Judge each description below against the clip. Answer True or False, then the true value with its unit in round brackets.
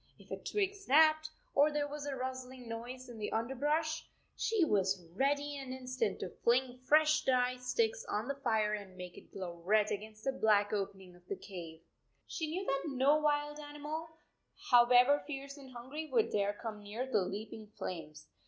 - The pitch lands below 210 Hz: False (255 Hz)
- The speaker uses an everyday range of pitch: False (5.7 semitones)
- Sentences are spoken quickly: False (190 wpm)